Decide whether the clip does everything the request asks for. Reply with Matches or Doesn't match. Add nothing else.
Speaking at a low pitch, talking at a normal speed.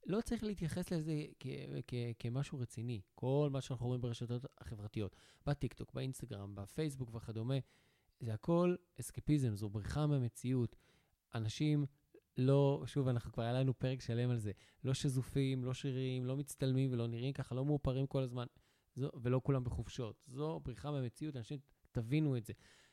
Doesn't match